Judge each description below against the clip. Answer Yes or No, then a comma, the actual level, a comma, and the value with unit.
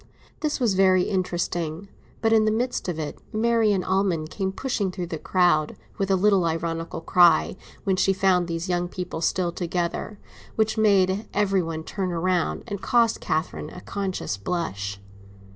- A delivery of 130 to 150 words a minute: No, average, 160 wpm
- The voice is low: No, medium, 185 Hz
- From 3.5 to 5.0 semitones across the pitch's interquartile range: No, average, 3.0 semitones